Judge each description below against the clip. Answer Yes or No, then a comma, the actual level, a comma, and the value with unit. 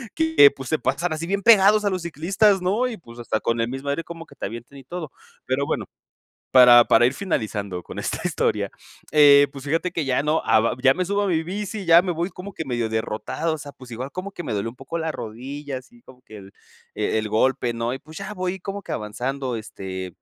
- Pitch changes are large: Yes, wide, 7.1 semitones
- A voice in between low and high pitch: Yes, medium, 145 Hz